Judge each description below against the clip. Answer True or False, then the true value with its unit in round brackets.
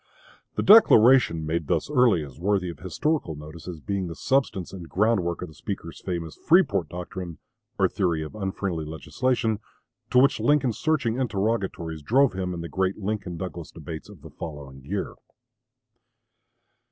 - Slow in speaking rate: False (155 wpm)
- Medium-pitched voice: False (95 Hz)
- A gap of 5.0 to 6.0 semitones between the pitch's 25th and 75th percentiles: True (5.5 semitones)